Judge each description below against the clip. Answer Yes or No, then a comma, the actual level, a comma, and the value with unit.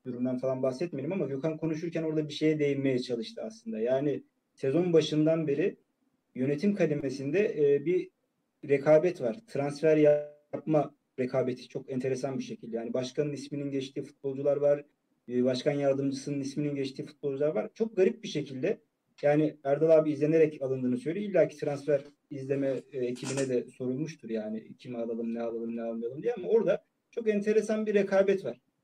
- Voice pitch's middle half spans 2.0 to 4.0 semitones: Yes, average, 3.6 semitones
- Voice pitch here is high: No, medium, 145 Hz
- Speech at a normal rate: No, fast, 150 wpm